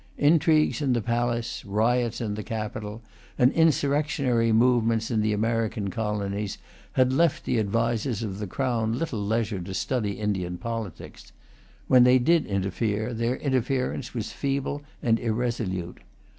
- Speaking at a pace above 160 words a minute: No, average, 140 wpm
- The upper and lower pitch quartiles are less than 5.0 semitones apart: Yes, average, 3.1 semitones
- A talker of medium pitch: No, low, 115 Hz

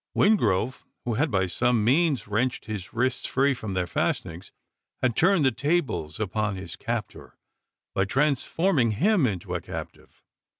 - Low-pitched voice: Yes, low, 120 Hz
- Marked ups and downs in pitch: Yes, wide, 6.0 semitones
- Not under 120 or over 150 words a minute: Yes, average, 145 wpm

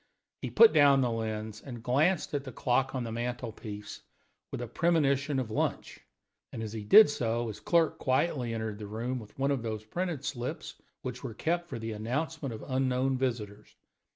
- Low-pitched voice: Yes, low, 125 Hz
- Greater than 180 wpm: Yes, average, 190 wpm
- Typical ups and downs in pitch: Yes, average, 3.8 semitones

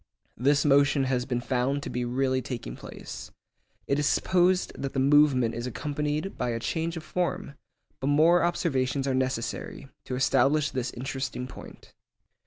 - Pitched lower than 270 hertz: Yes, low, 135 Hz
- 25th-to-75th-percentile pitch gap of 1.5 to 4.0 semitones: Yes, average, 2.8 semitones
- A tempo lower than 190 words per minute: Yes, average, 160 wpm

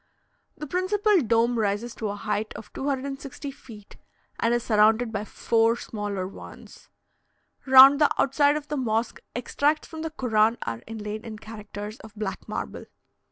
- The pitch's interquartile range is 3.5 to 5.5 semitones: Yes, average, 4.5 semitones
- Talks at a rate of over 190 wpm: No, average, 155 wpm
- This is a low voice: No, high, 230 Hz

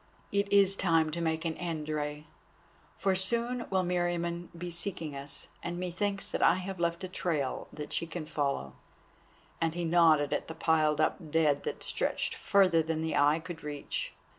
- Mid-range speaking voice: Yes, medium, 165 Hz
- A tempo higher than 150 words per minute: Yes, average, 180 wpm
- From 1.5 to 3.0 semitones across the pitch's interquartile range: Yes, average, 2.7 semitones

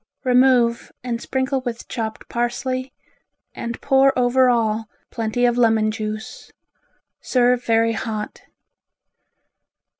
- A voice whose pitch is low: No, high, 240 Hz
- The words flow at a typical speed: No, slow, 100 wpm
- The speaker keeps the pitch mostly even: Yes, narrow, 2.1 semitones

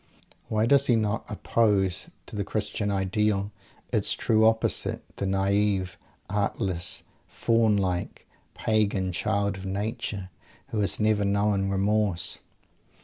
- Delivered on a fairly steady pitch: Yes, narrow, 1.9 semitones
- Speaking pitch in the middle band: No, low, 100 Hz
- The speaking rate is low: Yes, slow, 120 wpm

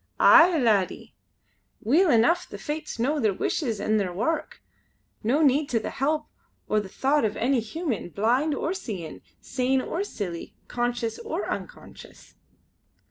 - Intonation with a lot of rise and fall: Yes, wide, 5.9 semitones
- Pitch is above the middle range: Yes, very high, 250 Hz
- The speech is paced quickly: No, average, 145 wpm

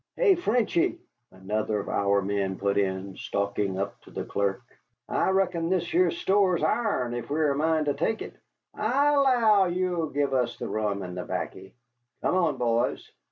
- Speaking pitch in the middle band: Yes, medium, 145 Hz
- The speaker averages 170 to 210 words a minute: Yes, average, 175 wpm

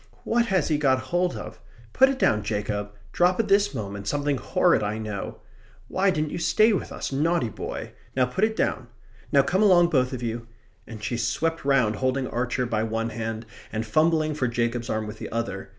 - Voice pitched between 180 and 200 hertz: No, low, 130 Hz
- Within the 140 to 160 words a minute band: No, fast, 205 wpm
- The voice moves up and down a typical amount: No, wide, 7.3 semitones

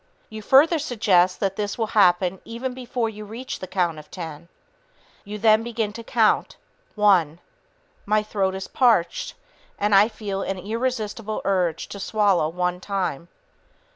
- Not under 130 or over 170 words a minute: Yes, average, 150 wpm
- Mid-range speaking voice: No, high, 205 Hz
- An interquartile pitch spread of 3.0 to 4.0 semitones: Yes, average, 3.5 semitones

